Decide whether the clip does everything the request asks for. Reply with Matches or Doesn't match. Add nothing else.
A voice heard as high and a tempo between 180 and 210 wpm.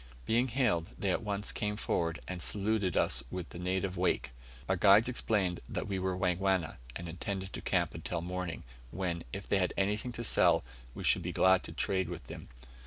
Doesn't match